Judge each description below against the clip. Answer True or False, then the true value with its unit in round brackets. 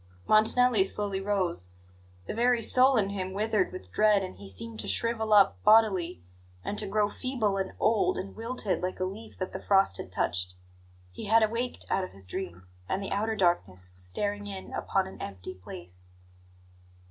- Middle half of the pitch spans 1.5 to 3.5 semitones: False (4.1 semitones)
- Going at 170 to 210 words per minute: True (180 wpm)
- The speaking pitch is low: False (195 Hz)